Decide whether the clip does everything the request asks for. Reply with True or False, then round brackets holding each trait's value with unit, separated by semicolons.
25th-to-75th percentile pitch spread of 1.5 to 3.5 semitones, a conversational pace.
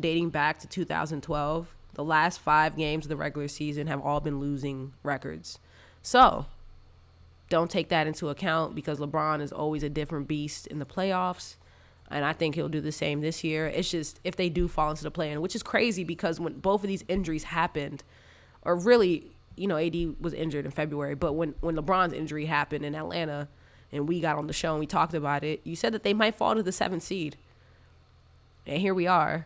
False (2.6 semitones; 210 wpm)